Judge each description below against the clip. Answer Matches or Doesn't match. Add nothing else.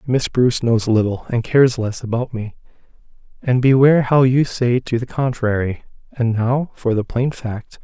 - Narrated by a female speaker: Doesn't match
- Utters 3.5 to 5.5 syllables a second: Matches